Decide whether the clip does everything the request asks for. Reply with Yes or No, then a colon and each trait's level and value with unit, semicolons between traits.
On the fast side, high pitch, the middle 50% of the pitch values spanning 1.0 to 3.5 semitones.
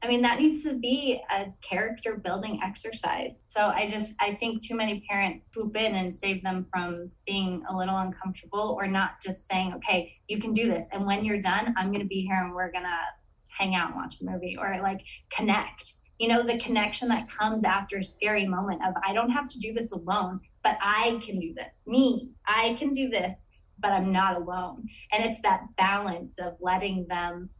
Yes: fast, 215 wpm; high, 200 Hz; average, 3.2 semitones